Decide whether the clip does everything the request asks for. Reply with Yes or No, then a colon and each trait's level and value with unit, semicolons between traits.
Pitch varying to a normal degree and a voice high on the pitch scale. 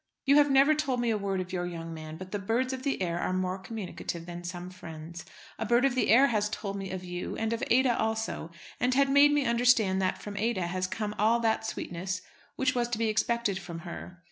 Yes: average, 4.8 semitones; high, 210 Hz